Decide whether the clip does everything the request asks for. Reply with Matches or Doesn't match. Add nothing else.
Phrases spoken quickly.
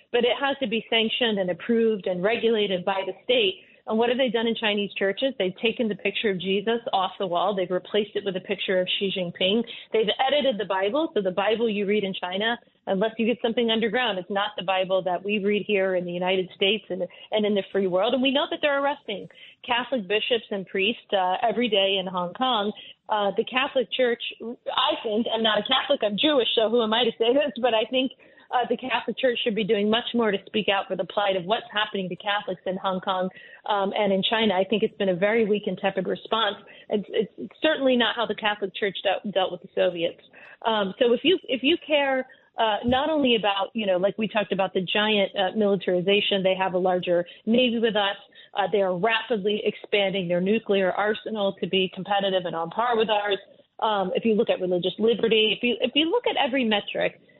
Matches